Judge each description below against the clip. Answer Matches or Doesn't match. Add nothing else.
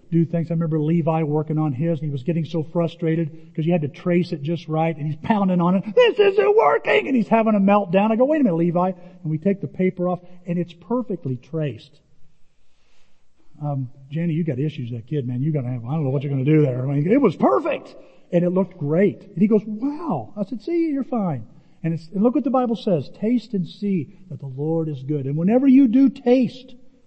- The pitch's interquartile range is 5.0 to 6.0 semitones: Matches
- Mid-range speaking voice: Matches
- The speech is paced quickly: Matches